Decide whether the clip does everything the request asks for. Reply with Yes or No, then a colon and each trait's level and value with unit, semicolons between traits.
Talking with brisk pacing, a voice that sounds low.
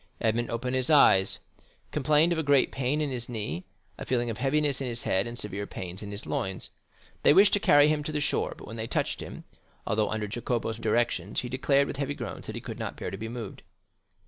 Yes: fast, 225 wpm; low, 120 Hz